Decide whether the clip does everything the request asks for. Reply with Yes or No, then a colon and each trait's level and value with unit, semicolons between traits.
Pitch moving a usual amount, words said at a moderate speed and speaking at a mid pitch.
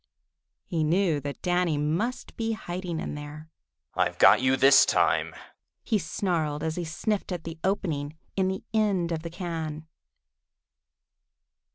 Yes: average, 3.5 semitones; average, 145 wpm; medium, 165 Hz